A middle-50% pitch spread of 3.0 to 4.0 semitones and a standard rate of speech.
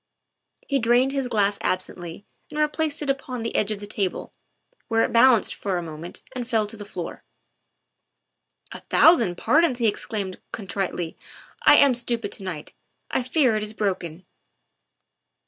No: average, 4.7 semitones; average, 165 wpm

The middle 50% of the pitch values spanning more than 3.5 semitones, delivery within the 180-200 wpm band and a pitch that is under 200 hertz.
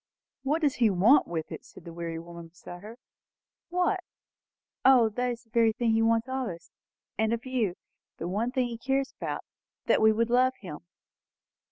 No: wide, 5.5 semitones; average, 195 wpm; high, 230 Hz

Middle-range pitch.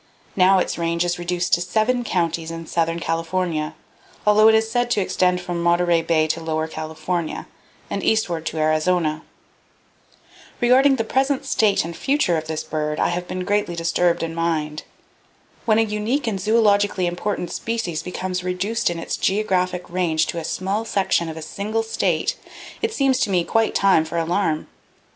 Yes: medium, 180 Hz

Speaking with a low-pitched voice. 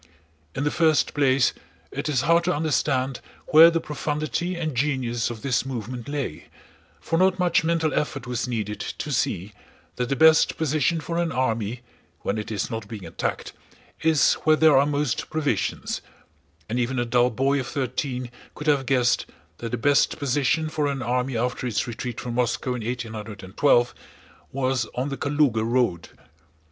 Yes: low, 130 Hz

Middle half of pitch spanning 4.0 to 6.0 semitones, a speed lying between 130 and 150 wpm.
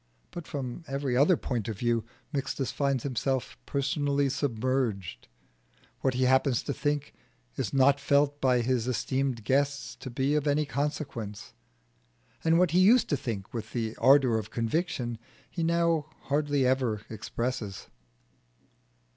No: average, 3.4 semitones; average, 140 wpm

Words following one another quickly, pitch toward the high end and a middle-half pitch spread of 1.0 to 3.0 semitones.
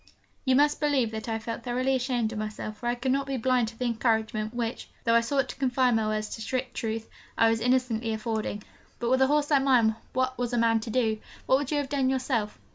Yes: fast, 245 wpm; high, 240 Hz; average, 2.7 semitones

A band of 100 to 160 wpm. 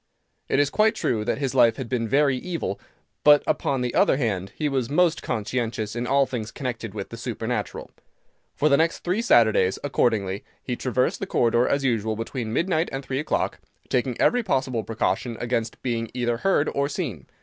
No: average, 185 wpm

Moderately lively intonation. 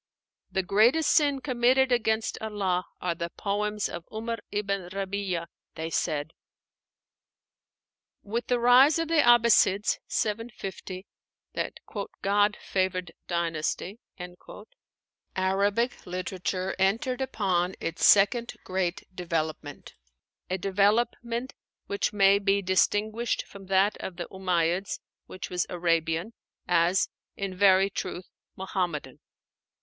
Yes: average, 3.4 semitones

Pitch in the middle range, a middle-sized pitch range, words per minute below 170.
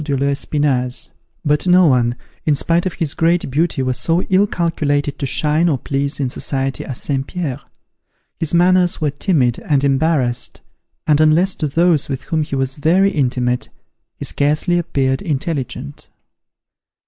Yes: medium, 145 Hz; average, 3.7 semitones; average, 155 wpm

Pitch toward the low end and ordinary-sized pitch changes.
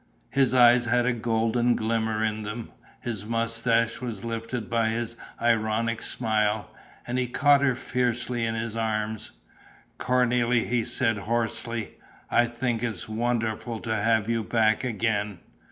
No: low, 115 Hz; narrow, 1.5 semitones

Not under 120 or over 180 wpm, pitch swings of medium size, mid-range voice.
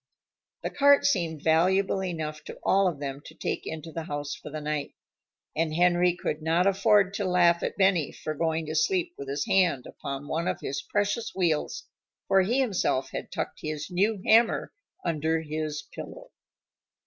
Yes: average, 175 wpm; average, 3.9 semitones; medium, 165 Hz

